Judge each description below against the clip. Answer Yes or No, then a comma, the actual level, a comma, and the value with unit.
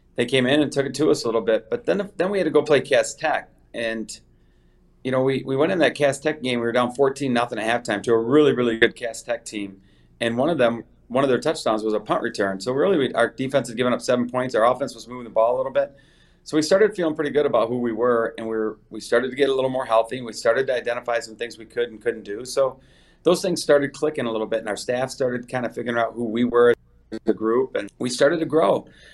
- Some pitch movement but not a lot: Yes, average, 3.8 semitones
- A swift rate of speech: Yes, fast, 280 wpm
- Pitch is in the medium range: No, low, 125 Hz